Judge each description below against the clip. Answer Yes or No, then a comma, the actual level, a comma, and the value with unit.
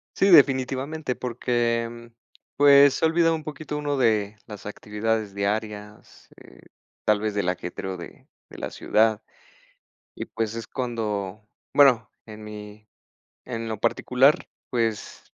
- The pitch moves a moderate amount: Yes, average, 3.8 semitones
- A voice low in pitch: Yes, low, 115 Hz